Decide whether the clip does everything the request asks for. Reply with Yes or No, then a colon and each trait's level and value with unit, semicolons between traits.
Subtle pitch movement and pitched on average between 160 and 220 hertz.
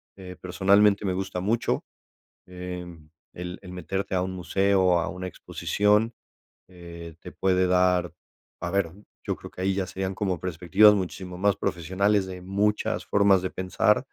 No: narrow, 1.6 semitones; very low, 95 Hz